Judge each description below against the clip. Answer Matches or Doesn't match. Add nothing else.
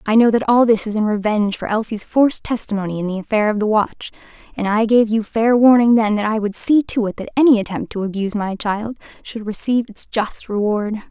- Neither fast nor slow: Doesn't match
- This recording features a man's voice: Doesn't match